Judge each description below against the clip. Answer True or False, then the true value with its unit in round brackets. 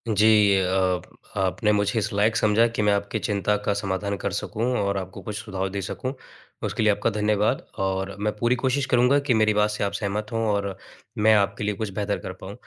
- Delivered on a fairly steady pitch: True (1.6 semitones)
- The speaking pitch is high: False (105 Hz)